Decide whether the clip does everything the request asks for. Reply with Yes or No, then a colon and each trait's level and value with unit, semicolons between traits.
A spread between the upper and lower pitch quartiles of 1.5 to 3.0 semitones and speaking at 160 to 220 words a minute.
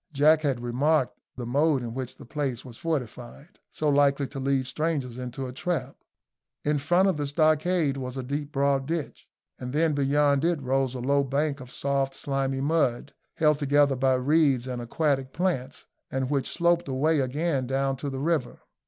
Yes: narrow, 2.6 semitones; average, 180 wpm